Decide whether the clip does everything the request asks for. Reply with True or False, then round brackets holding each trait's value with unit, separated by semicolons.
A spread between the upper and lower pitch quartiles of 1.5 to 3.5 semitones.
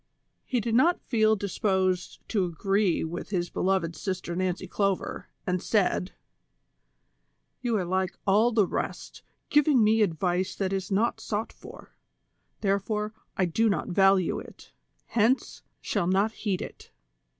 True (2.8 semitones)